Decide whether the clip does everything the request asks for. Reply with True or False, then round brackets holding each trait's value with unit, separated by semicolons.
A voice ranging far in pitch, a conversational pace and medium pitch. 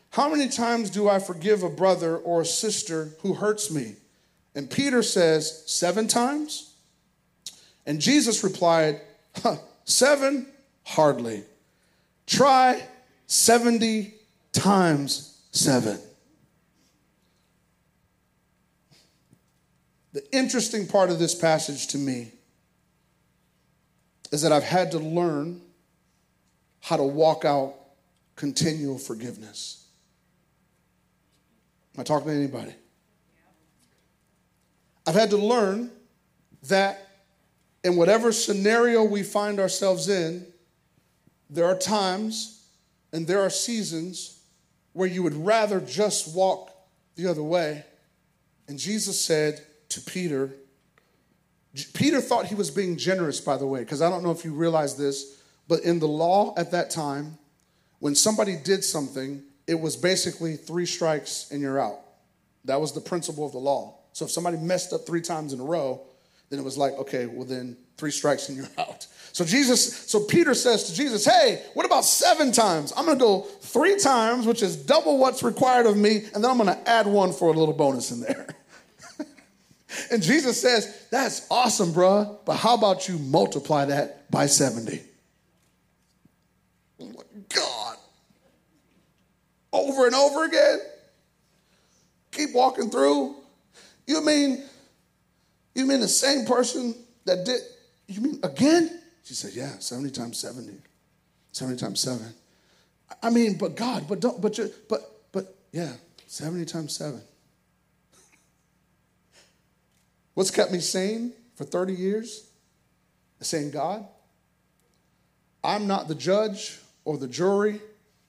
False (6.4 semitones; 130 wpm; 180 Hz)